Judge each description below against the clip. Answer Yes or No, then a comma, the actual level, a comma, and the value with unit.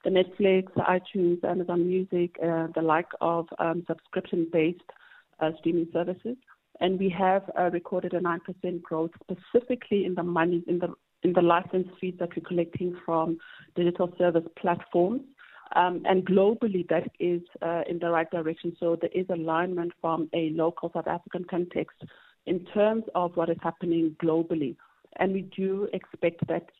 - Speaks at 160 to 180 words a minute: Yes, average, 165 wpm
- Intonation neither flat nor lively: No, narrow, 1.7 semitones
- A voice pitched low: No, medium, 175 Hz